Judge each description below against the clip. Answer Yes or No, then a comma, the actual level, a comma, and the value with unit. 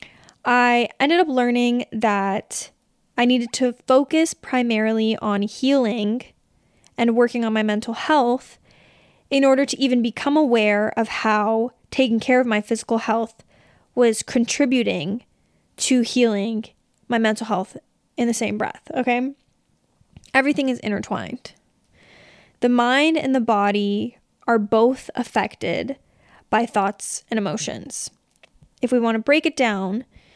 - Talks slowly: Yes, slow, 130 wpm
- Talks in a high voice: Yes, high, 235 Hz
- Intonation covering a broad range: No, average, 2.8 semitones